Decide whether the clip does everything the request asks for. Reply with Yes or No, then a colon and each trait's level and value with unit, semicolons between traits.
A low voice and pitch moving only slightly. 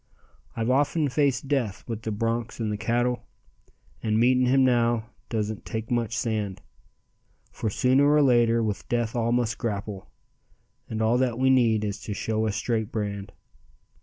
Yes: low, 115 Hz; narrow, 2.3 semitones